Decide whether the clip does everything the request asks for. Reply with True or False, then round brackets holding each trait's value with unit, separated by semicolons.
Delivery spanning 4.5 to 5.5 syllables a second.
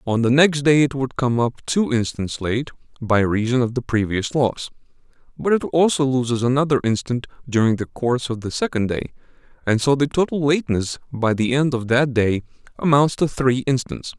True (5.3 syllables/s)